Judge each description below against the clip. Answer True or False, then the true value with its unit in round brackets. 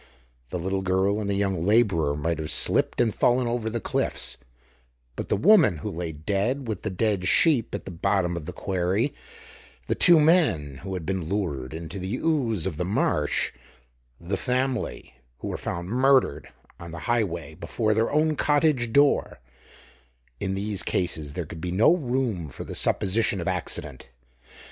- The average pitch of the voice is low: True (95 Hz)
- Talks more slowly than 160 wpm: False (170 wpm)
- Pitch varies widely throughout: True (5.9 semitones)